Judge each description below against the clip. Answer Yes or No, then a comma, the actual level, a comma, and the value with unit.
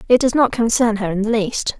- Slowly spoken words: No, fast, 270 wpm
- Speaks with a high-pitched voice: Yes, high, 225 Hz